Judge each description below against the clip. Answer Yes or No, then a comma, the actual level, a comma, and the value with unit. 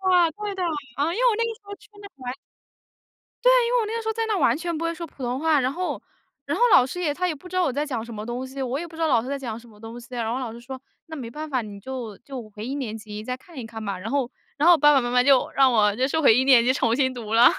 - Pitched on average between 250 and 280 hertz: Yes, very high, 265 Hz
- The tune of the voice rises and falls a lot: Yes, wide, 5.8 semitones